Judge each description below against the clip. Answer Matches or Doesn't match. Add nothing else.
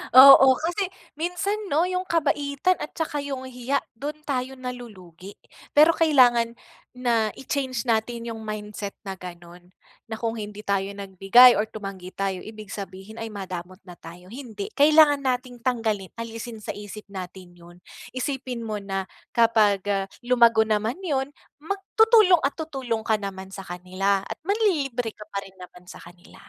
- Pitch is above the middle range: Matches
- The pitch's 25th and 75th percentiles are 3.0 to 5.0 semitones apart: Doesn't match